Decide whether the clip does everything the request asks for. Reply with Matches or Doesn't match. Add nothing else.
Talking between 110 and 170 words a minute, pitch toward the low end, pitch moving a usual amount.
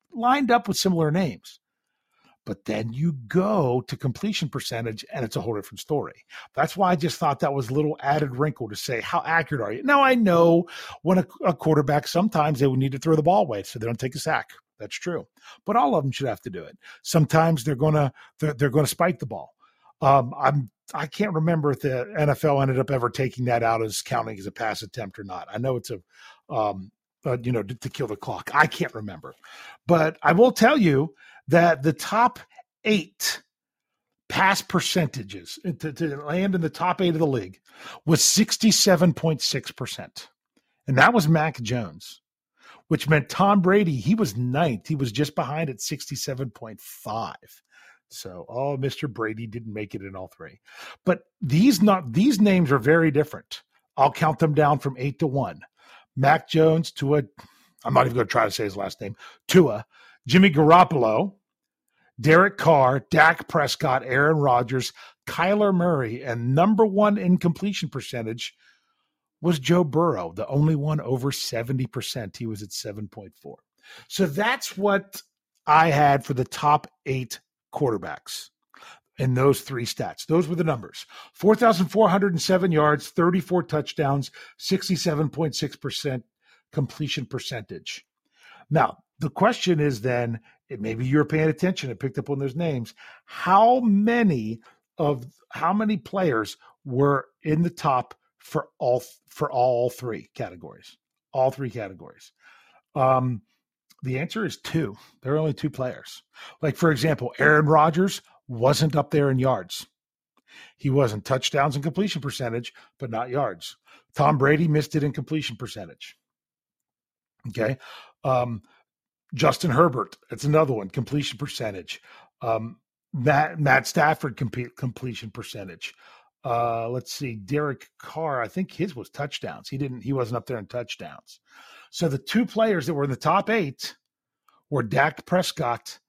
Doesn't match